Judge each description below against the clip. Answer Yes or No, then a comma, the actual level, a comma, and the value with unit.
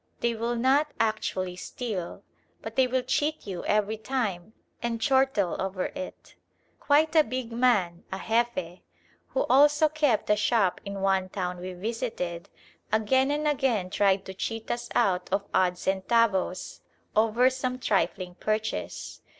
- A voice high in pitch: Yes, high, 220 Hz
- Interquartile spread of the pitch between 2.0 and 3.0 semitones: No, average, 5.2 semitones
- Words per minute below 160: Yes, average, 145 wpm